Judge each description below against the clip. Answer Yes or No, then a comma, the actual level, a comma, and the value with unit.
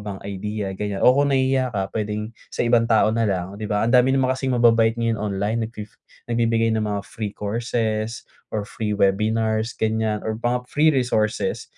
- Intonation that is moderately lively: No, narrow, 2.1 semitones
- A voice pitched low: Yes, low, 110 Hz